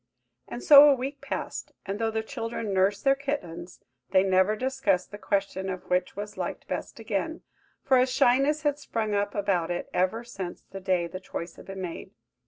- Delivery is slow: No, average, 190 wpm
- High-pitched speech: Yes, high, 205 Hz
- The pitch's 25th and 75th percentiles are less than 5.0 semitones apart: No, wide, 5.4 semitones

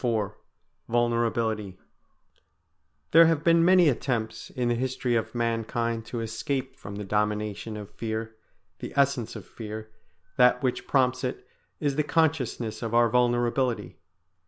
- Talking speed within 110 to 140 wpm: Yes, slow, 135 wpm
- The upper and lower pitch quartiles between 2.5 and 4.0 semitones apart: Yes, average, 2.8 semitones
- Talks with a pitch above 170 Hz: No, low, 120 Hz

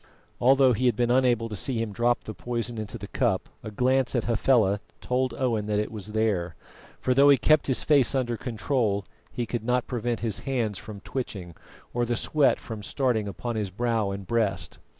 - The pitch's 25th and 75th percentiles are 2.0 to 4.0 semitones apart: Yes, average, 3.1 semitones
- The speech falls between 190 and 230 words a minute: Yes, average, 200 wpm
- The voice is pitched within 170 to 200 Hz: No, low, 115 Hz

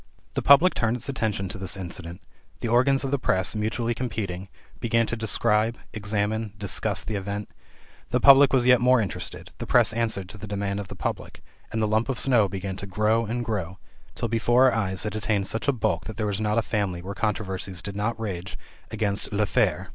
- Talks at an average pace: No, fast, 210 wpm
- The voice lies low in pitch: Yes, low, 110 Hz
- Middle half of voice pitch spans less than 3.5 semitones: Yes, average, 2.8 semitones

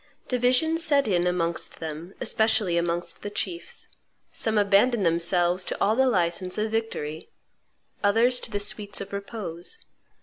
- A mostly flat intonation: No, average, 4.5 semitones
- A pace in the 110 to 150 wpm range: Yes, average, 140 wpm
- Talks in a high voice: Yes, high, 200 Hz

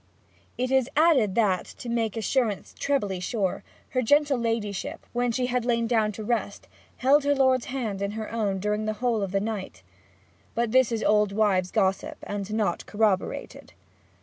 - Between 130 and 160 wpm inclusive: No, average, 175 wpm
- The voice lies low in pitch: No, high, 220 Hz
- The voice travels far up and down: No, average, 3.4 semitones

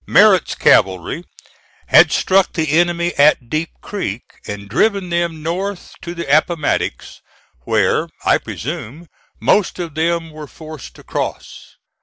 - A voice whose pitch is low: No, medium, 165 Hz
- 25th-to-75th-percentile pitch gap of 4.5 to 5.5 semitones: No, average, 2.7 semitones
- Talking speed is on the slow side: Yes, slow, 130 wpm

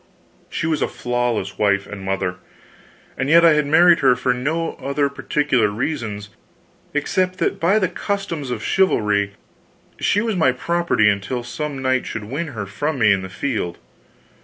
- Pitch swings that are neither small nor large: No, wide, 7.3 semitones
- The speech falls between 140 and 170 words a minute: Yes, average, 165 wpm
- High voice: No, low, 130 Hz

